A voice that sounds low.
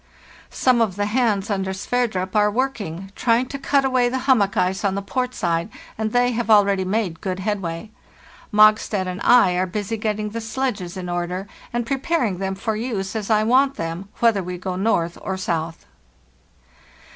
No: high, 210 Hz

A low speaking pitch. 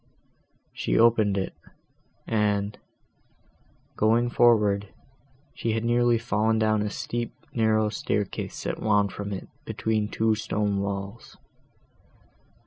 Yes: low, 110 Hz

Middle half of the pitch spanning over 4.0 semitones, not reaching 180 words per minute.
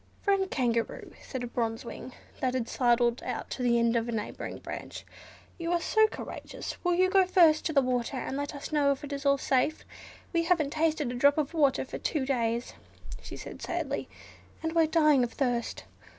No: average, 4.8 semitones; fast, 205 wpm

